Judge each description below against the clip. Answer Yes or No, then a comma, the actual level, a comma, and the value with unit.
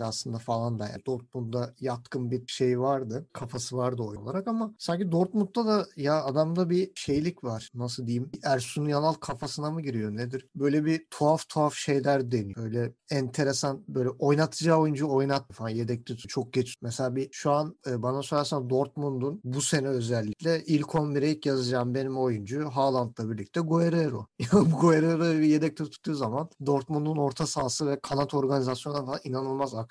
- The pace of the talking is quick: Yes, fast, 165 wpm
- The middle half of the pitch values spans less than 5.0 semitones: Yes, average, 3.6 semitones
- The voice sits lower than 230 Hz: Yes, medium, 140 Hz